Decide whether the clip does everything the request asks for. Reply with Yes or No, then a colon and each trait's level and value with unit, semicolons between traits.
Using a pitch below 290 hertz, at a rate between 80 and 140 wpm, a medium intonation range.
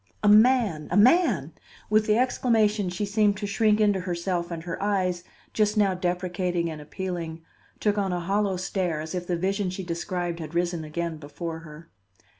No: medium, 185 Hz; average, 180 wpm; average, 3.3 semitones